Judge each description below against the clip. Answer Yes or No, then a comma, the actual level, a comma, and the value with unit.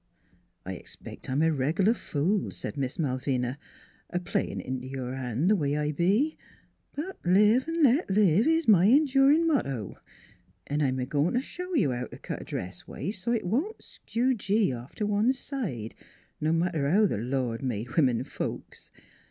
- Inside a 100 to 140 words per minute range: No, average, 190 wpm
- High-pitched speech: No, medium, 165 Hz